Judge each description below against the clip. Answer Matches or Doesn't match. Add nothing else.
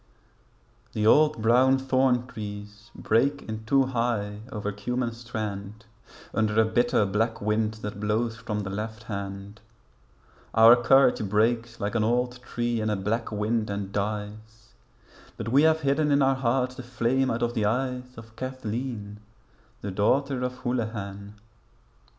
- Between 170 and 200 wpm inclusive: Doesn't match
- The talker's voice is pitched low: Matches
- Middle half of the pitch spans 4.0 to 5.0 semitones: Doesn't match